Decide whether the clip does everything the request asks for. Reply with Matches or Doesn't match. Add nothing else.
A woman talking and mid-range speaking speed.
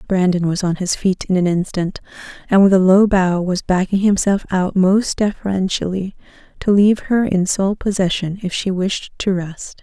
Matches